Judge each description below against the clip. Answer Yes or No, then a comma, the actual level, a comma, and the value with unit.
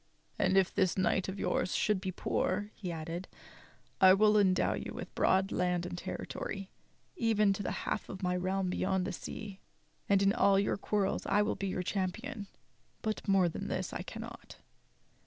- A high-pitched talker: Yes, high, 195 Hz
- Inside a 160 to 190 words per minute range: Yes, average, 185 wpm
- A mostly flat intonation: Yes, narrow, 1.7 semitones